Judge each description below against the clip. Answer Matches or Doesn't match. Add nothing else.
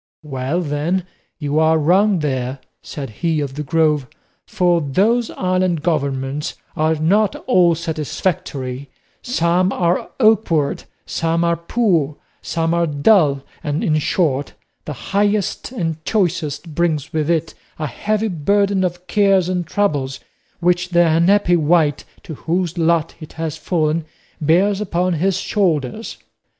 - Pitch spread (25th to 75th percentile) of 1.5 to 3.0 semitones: Doesn't match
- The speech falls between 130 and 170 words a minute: Matches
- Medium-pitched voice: Matches